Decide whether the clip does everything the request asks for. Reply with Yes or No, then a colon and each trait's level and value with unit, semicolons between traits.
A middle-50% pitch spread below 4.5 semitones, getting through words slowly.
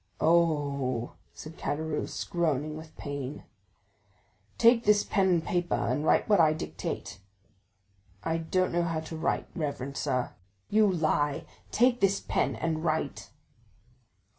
Yes: average, 3.2 semitones; slow, 130 wpm